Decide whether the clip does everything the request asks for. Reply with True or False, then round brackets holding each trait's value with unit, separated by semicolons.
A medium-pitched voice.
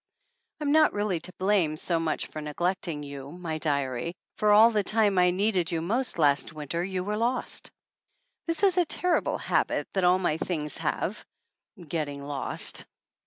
True (180 Hz)